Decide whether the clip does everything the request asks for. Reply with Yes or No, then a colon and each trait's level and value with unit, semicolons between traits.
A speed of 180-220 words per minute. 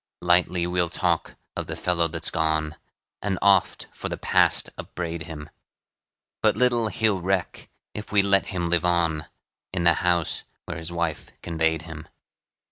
No: average, 155 wpm